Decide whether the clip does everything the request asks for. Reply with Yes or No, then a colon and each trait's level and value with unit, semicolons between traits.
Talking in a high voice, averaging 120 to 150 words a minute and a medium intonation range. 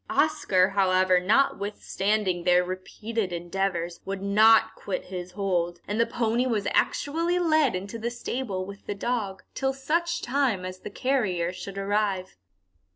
Yes: high, 200 Hz; average, 145 wpm; average, 4.5 semitones